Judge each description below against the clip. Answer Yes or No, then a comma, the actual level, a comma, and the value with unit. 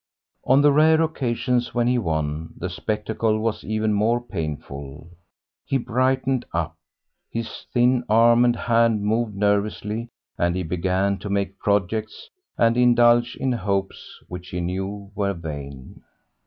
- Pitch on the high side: No, low, 105 Hz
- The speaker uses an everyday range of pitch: Yes, average, 4.5 semitones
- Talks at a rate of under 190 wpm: Yes, average, 140 wpm